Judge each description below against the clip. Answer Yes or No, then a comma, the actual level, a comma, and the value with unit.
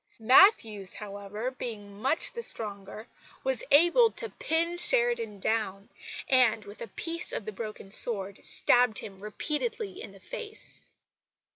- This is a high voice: Yes, high, 230 Hz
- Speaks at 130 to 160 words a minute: Yes, slow, 135 wpm